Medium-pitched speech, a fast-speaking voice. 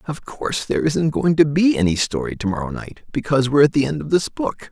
Yes: medium, 145 Hz; fast, 255 wpm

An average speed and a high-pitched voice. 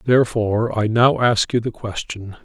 No: average, 170 wpm; low, 115 Hz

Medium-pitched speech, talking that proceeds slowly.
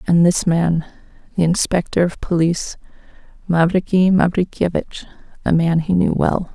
Yes: medium, 170 Hz; slow, 120 wpm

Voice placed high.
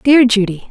Yes: high, 230 Hz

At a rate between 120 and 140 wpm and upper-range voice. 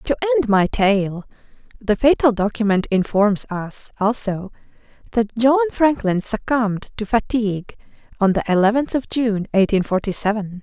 Yes: slow, 135 wpm; high, 215 Hz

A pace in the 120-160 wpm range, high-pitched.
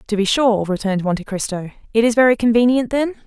No: average, 200 wpm; high, 220 Hz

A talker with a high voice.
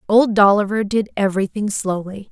Yes: high, 205 Hz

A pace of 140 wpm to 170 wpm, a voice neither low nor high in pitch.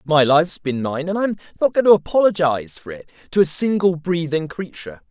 No: average, 200 wpm; medium, 165 Hz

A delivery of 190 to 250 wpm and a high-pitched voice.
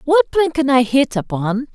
Yes: fast, 205 wpm; very high, 275 Hz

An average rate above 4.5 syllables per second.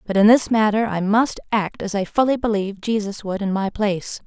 Yes: 5.5 syllables/s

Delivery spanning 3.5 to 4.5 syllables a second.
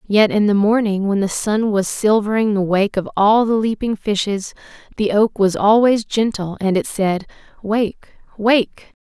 Yes: 4.4 syllables/s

